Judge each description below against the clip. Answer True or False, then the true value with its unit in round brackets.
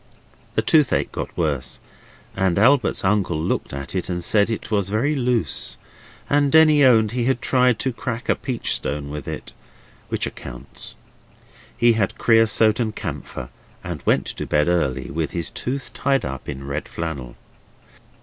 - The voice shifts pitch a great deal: True (8.5 semitones)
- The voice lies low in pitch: True (105 Hz)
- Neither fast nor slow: True (160 wpm)